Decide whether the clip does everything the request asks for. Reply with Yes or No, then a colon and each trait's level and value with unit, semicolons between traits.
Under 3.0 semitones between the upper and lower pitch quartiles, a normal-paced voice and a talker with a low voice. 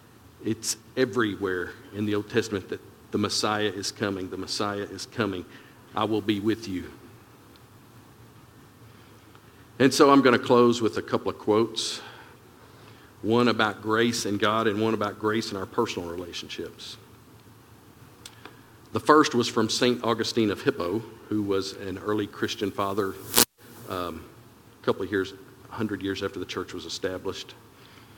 Yes: narrow, 2.5 semitones; average, 150 wpm; low, 110 Hz